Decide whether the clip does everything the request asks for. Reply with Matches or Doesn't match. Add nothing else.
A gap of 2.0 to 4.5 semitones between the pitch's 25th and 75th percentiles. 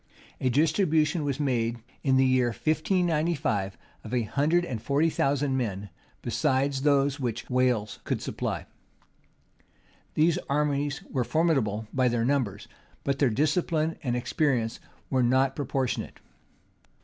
Matches